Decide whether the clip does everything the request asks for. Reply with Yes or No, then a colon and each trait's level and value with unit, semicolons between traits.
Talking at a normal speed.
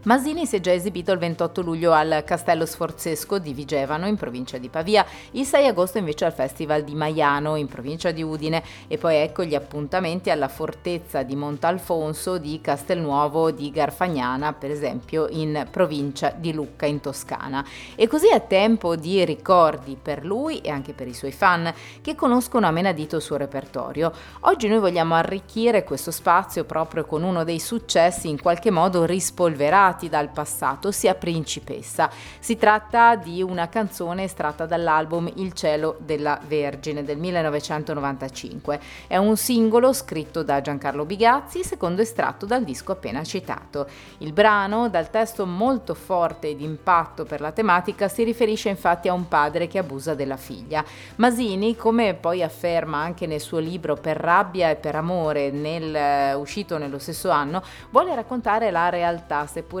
Yes: average, 160 wpm